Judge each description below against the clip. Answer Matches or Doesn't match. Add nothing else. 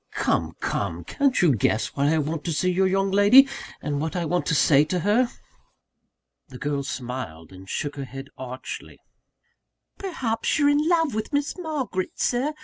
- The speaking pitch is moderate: Matches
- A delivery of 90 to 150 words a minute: Doesn't match